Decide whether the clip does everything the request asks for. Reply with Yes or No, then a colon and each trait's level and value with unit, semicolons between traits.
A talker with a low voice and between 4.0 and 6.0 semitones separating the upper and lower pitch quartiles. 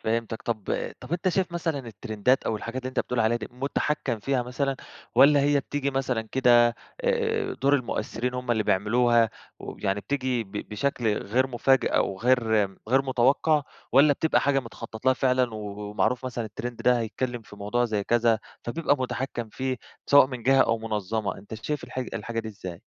No: low, 125 Hz; average, 3.3 semitones